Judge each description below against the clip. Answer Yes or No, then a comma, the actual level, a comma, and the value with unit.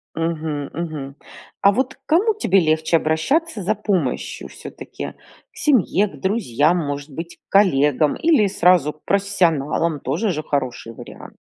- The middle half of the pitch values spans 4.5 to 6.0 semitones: Yes, average, 5.3 semitones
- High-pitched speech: No, medium, 170 Hz